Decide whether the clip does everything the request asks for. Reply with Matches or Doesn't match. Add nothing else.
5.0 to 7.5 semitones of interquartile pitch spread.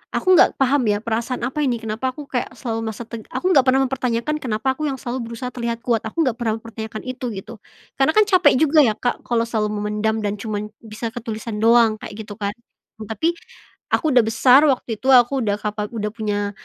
Doesn't match